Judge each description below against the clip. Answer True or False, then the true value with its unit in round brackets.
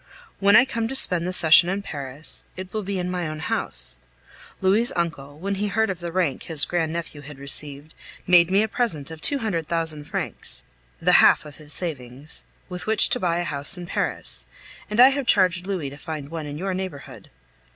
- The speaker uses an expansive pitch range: False (4.4 semitones)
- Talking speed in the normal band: False (210 wpm)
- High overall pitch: False (170 Hz)